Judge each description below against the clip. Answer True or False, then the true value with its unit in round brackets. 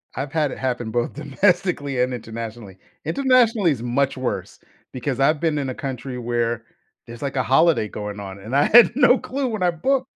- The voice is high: False (135 Hz)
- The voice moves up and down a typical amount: False (5.9 semitones)